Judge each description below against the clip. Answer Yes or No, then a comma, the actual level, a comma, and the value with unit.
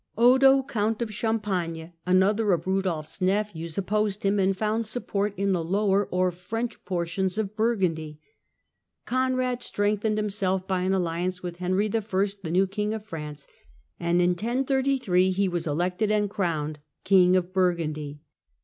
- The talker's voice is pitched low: No, high, 190 Hz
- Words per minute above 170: No, average, 150 wpm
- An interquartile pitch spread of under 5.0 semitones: Yes, average, 3.2 semitones